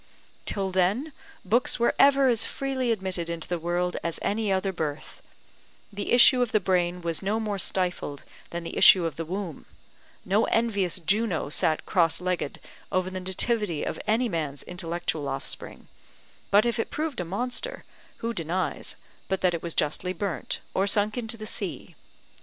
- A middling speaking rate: Yes, average, 170 wpm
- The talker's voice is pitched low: No, high, 190 Hz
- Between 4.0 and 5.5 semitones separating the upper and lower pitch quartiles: Yes, average, 4.5 semitones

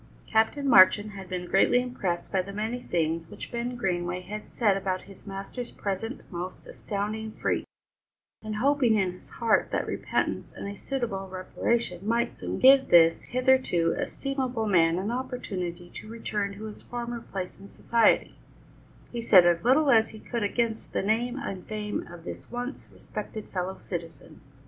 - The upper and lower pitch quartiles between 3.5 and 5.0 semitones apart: Yes, average, 4.4 semitones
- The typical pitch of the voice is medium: No, high, 210 Hz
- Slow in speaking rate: No, average, 165 wpm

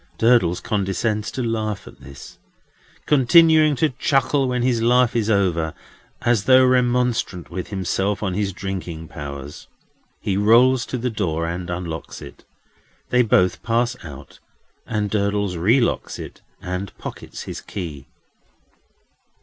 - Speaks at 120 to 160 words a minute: Yes, slow, 135 wpm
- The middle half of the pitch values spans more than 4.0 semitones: Yes, average, 5.3 semitones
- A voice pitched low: Yes, low, 105 Hz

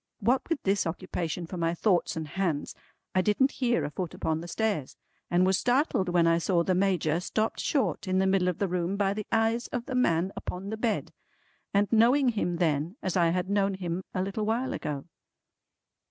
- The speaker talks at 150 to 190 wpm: No, fast, 205 wpm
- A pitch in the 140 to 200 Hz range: Yes, high, 190 Hz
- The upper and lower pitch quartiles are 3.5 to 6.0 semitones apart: Yes, average, 4.1 semitones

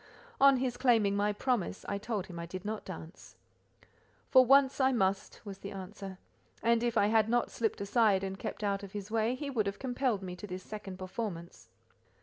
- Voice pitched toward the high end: Yes, high, 210 Hz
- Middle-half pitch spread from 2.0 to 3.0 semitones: No, average, 3.7 semitones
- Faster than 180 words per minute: Yes, average, 200 wpm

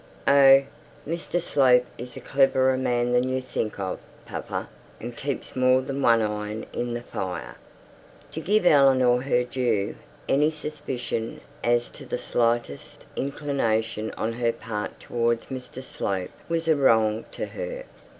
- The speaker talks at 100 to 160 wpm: Yes, average, 145 wpm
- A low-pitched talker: Yes, low, 125 Hz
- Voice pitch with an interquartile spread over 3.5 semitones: No, average, 3.0 semitones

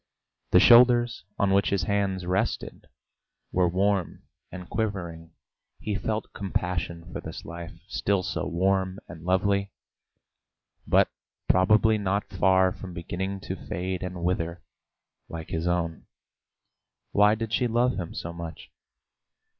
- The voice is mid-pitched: No, very low, 95 Hz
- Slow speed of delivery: Yes, slow, 130 wpm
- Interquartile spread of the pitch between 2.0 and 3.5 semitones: Yes, narrow, 2.5 semitones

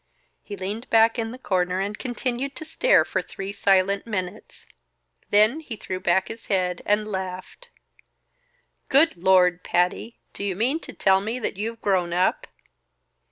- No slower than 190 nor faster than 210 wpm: No, average, 160 wpm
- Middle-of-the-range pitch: No, high, 200 Hz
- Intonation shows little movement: No, average, 3.7 semitones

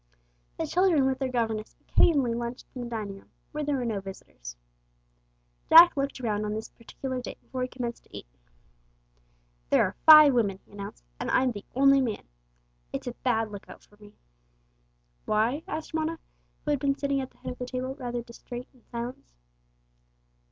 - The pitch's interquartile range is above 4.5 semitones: No, average, 3.8 semitones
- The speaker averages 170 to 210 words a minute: Yes, average, 180 wpm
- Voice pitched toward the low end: No, very high, 250 Hz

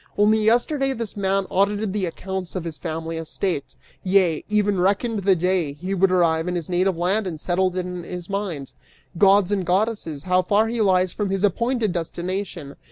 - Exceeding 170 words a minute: Yes, average, 185 wpm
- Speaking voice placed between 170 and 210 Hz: Yes, high, 190 Hz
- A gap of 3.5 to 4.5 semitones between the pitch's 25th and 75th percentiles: No, average, 2.7 semitones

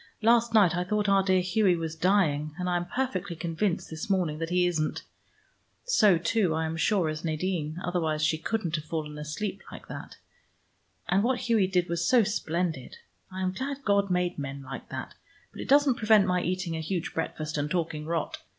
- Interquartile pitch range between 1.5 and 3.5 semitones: No, average, 4.0 semitones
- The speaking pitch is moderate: Yes, medium, 180 Hz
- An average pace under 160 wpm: No, average, 195 wpm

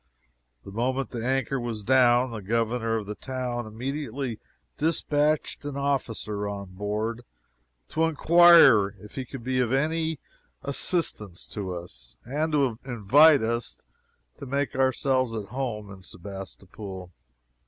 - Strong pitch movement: No, average, 4.5 semitones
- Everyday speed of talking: No, slow, 130 wpm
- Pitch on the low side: Yes, low, 120 Hz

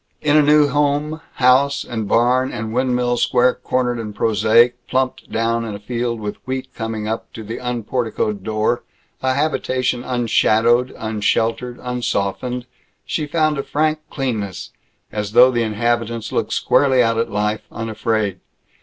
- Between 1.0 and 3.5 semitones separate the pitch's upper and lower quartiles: Yes, narrow, 2.6 semitones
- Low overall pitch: Yes, low, 120 Hz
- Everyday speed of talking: Yes, average, 145 wpm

